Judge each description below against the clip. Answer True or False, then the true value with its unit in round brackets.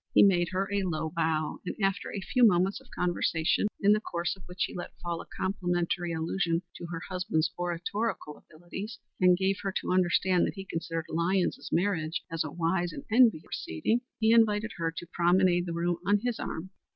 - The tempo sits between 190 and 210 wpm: True (195 wpm)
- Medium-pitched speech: True (180 Hz)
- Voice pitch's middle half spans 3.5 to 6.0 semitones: False (2.7 semitones)